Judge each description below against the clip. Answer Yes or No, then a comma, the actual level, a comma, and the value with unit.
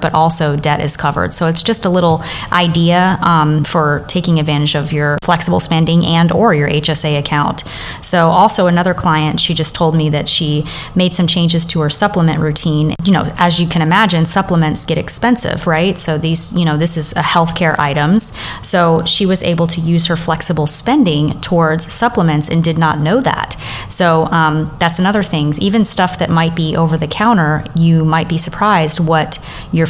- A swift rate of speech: No, average, 190 wpm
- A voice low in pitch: No, medium, 165 Hz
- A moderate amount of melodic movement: No, narrow, 2.1 semitones